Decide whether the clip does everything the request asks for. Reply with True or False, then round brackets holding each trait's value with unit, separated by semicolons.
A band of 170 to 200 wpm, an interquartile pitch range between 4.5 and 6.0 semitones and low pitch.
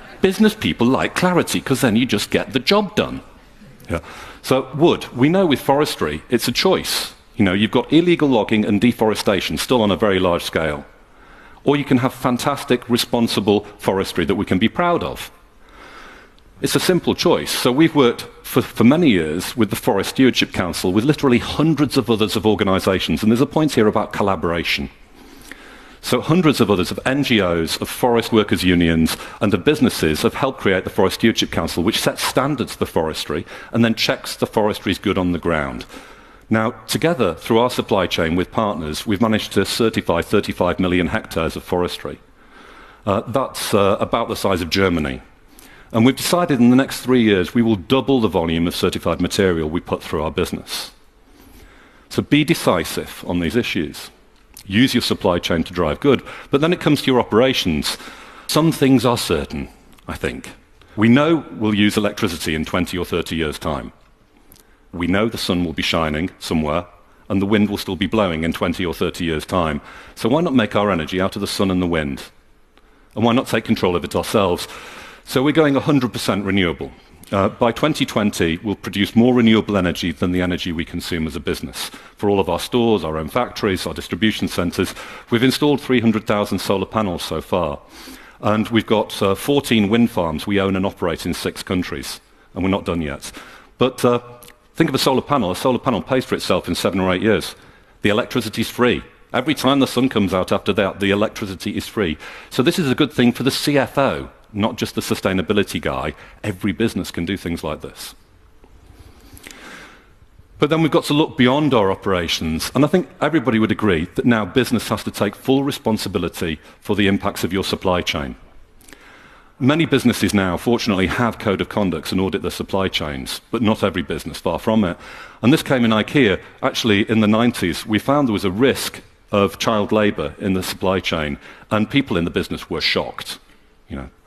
True (195 wpm; 5.1 semitones; 105 Hz)